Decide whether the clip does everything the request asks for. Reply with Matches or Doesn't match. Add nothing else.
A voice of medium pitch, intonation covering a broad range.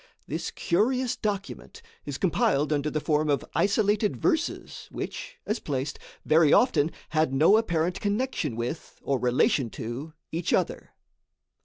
Matches